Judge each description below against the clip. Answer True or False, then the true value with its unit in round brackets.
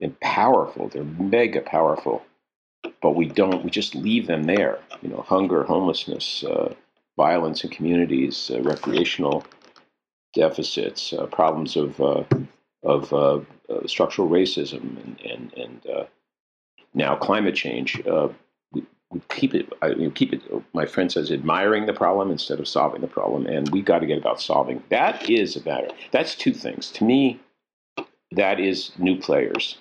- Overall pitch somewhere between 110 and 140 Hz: True (135 Hz)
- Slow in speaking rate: False (160 wpm)